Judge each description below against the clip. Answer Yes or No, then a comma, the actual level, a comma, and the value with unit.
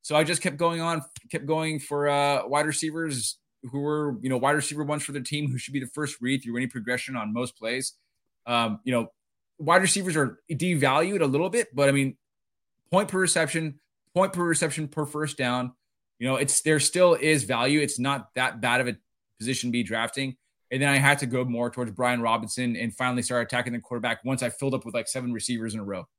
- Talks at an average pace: No, fast, 230 wpm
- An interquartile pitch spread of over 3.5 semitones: Yes, average, 3.9 semitones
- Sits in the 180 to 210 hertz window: No, low, 135 Hz